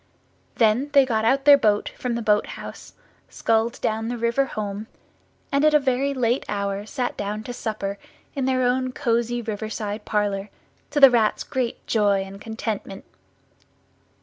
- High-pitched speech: Yes, high, 225 Hz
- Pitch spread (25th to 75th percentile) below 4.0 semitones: Yes, average, 3.5 semitones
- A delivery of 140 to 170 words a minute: Yes, average, 160 wpm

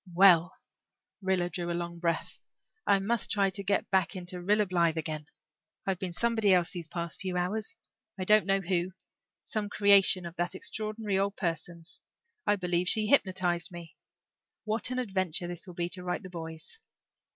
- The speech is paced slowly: No, average, 175 wpm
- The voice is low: No, medium, 185 Hz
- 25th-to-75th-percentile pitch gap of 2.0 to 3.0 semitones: Yes, narrow, 2.6 semitones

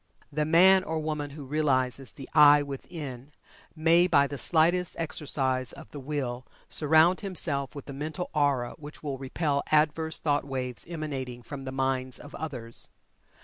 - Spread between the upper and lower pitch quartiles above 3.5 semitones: No, average, 2.9 semitones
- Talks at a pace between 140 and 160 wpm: Yes, average, 155 wpm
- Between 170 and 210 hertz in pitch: No, medium, 145 Hz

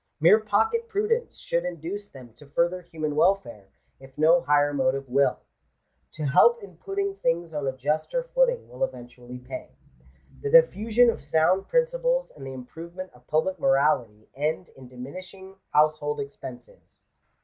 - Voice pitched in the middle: Yes, medium, 160 Hz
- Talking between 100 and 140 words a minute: No, average, 150 wpm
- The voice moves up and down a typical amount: No, wide, 7.8 semitones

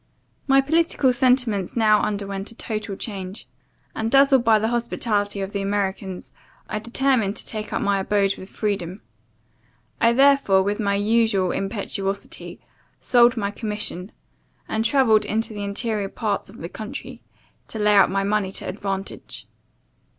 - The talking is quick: No, average, 150 wpm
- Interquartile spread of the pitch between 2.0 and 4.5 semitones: Yes, average, 2.8 semitones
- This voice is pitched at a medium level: No, high, 210 Hz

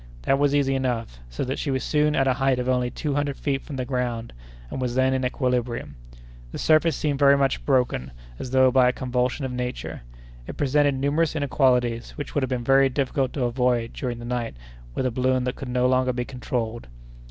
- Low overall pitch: Yes, low, 130 Hz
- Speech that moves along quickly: Yes, fast, 215 wpm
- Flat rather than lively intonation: Yes, narrow, 1.7 semitones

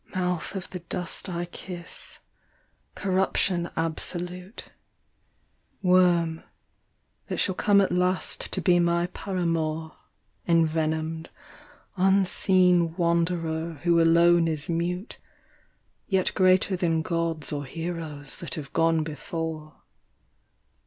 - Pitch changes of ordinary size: No, narrow, 2.0 semitones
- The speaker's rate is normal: No, slow, 105 wpm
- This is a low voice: No, medium, 170 Hz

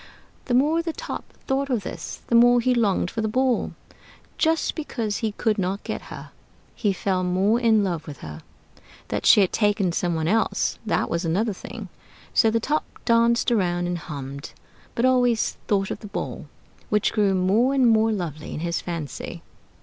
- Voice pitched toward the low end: No, high, 210 Hz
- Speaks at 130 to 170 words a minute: No, average, 185 wpm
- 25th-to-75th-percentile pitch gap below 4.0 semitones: No, average, 4.8 semitones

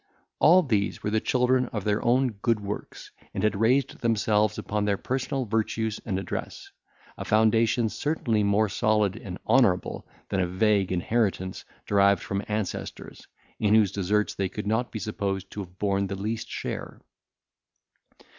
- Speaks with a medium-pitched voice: No, low, 105 Hz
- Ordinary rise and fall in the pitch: No, narrow, 2.3 semitones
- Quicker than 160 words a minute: No, average, 155 wpm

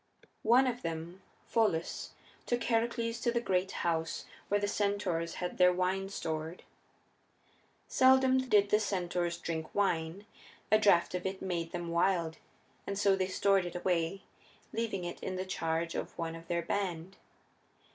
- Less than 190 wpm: Yes, average, 155 wpm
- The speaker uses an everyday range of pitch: Yes, average, 3.3 semitones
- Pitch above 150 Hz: Yes, medium, 185 Hz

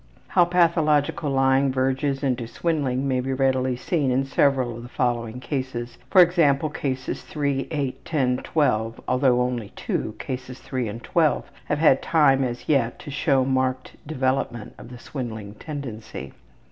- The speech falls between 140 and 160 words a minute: Yes, average, 150 wpm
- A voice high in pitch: No, low, 130 Hz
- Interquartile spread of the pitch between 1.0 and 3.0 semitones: Yes, narrow, 2.4 semitones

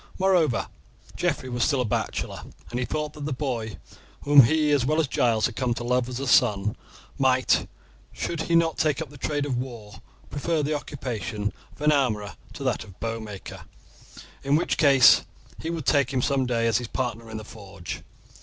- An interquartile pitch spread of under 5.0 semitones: Yes, average, 4.3 semitones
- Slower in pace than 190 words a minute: No, average, 200 wpm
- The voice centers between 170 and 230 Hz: No, low, 130 Hz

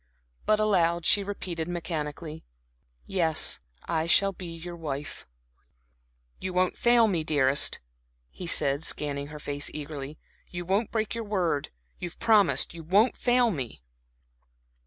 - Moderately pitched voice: Yes, medium, 170 Hz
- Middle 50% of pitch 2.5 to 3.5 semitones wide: No, average, 4.6 semitones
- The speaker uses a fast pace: No, slow, 135 wpm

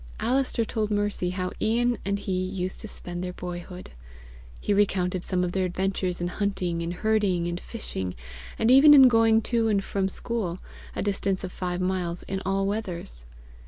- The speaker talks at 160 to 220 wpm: Yes, average, 175 wpm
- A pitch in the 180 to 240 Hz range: Yes, high, 190 Hz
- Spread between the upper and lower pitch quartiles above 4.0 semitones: No, average, 3.2 semitones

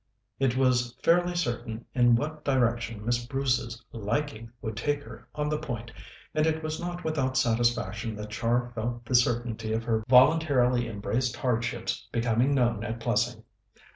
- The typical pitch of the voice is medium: No, low, 120 Hz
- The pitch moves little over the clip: No, average, 3.0 semitones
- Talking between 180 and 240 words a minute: No, average, 155 wpm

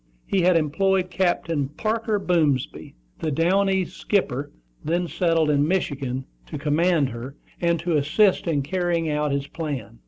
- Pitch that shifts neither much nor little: Yes, average, 4.1 semitones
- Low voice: No, medium, 165 Hz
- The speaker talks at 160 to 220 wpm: No, average, 150 wpm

